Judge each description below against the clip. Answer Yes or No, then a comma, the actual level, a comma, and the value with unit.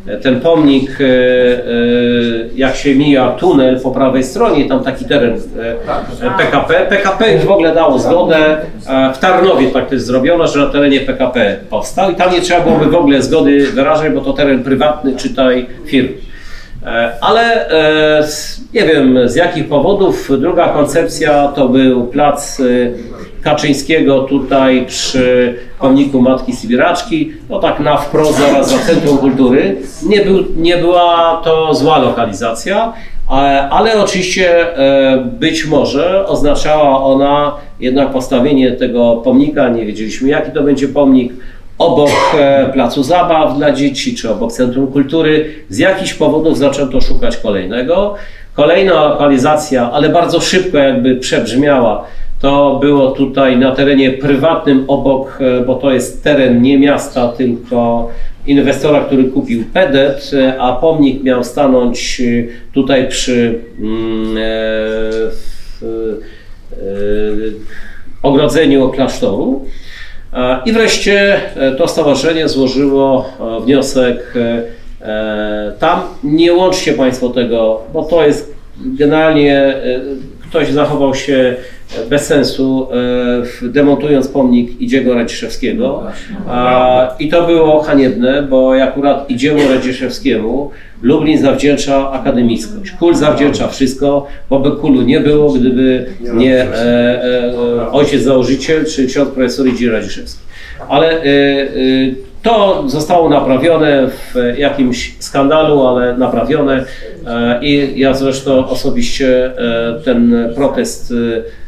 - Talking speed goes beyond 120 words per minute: No, average, 115 wpm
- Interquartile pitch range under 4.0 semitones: Yes, average, 3.0 semitones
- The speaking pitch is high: No, low, 135 Hz